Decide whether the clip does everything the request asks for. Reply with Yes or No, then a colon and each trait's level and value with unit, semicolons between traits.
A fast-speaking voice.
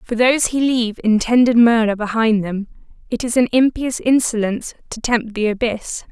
No: average, 165 wpm